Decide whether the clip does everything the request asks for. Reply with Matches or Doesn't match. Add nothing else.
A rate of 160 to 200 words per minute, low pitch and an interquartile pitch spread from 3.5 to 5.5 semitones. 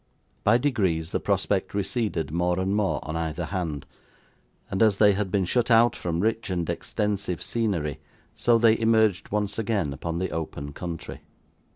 Matches